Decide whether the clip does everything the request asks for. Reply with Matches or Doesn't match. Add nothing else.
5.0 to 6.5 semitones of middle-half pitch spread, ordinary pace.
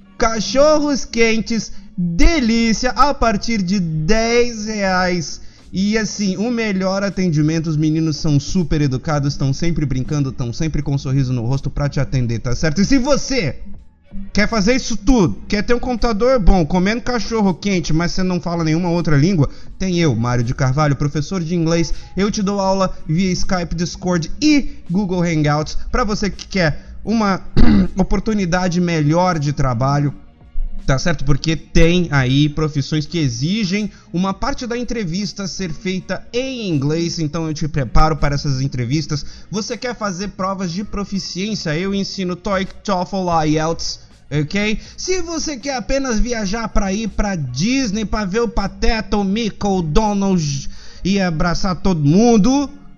Matches